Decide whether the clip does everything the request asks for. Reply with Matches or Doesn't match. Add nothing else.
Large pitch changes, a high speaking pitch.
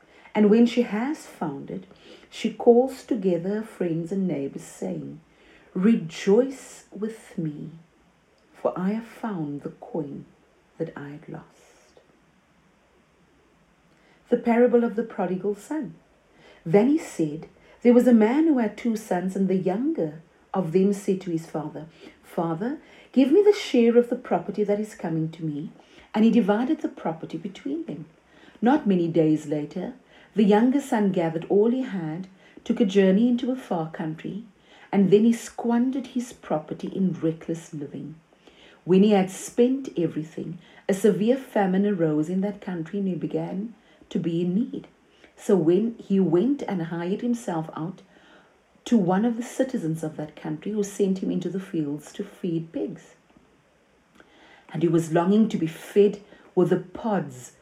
Matches